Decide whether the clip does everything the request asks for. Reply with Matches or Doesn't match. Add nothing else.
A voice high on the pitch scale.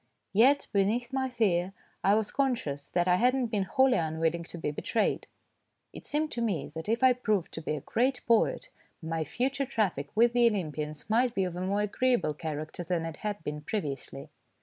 Matches